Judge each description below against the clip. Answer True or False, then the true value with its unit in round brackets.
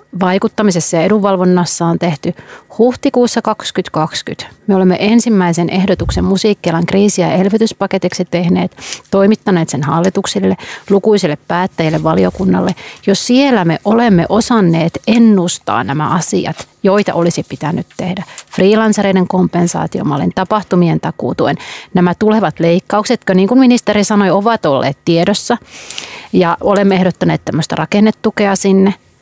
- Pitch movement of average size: True (3.3 semitones)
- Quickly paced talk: False (115 wpm)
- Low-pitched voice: False (190 Hz)